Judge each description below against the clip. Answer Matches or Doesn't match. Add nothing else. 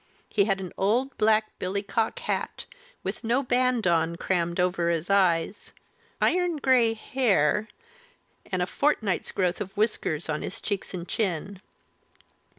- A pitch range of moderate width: Matches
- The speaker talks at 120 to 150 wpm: Matches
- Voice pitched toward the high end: Matches